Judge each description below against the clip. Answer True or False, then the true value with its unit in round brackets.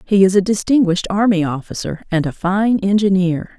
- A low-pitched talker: False (190 Hz)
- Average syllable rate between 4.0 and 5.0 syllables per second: False (5.3 syllables/s)